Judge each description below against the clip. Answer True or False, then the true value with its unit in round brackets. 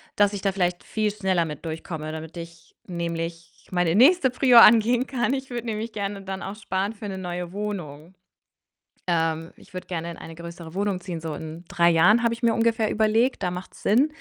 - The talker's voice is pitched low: False (190 Hz)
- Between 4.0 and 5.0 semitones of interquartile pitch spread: True (4.5 semitones)